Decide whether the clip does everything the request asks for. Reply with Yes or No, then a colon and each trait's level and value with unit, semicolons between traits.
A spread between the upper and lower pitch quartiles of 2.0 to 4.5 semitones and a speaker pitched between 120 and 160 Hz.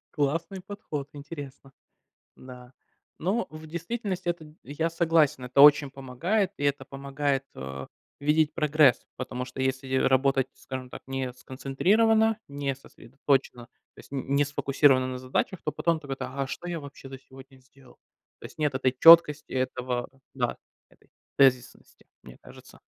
Yes: average, 3.1 semitones; medium, 140 Hz